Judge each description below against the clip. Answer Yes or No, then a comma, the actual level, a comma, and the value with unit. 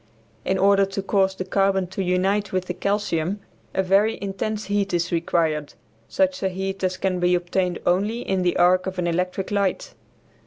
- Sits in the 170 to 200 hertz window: Yes, high, 190 Hz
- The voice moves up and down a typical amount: No, narrow, 1.7 semitones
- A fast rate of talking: No, average, 185 wpm